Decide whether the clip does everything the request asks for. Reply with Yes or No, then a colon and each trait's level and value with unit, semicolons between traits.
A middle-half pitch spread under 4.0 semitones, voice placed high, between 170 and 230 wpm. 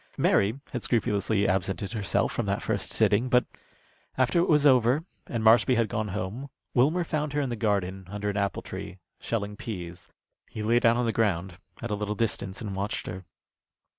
No: average, 3.5 semitones; low, 110 Hz; average, 190 wpm